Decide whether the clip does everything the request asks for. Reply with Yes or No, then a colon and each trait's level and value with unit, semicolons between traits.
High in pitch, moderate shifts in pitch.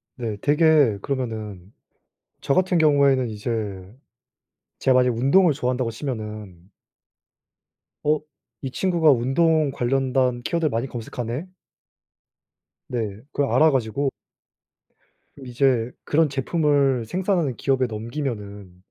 No: low, 130 Hz; average, 4.5 semitones